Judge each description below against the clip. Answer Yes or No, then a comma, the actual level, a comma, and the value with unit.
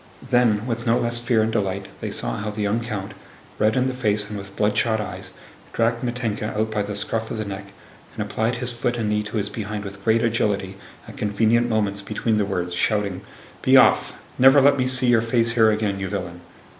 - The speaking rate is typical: No, fast, 220 wpm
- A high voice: No, low, 110 Hz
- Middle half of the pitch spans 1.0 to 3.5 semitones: Yes, narrow, 2.4 semitones